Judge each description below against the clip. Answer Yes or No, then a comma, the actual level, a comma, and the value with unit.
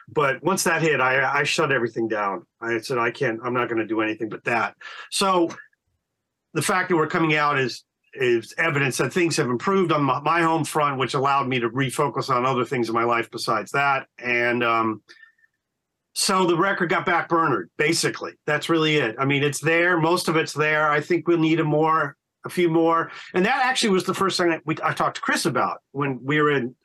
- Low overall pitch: No, medium, 155 Hz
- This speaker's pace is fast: Yes, fast, 225 wpm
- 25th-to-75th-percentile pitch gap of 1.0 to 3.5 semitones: No, average, 4.6 semitones